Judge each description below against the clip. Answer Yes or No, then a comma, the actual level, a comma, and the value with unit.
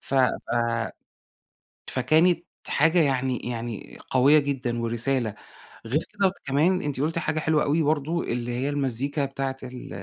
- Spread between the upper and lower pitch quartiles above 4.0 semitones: No, average, 3.6 semitones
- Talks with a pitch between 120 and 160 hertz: Yes, low, 135 Hz